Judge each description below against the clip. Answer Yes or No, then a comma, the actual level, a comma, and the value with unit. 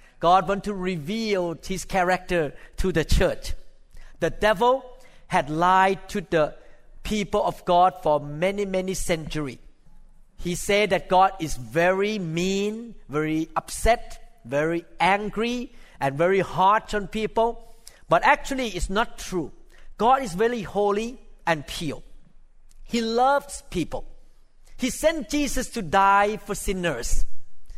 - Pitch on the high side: Yes, high, 195 Hz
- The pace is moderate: No, slow, 125 wpm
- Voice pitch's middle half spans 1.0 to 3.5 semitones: No, average, 4.8 semitones